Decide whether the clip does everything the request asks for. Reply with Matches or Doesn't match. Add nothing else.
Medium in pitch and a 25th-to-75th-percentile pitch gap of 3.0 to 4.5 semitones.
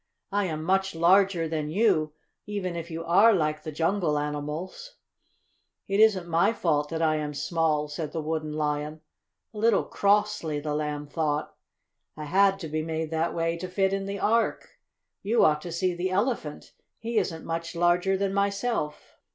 Matches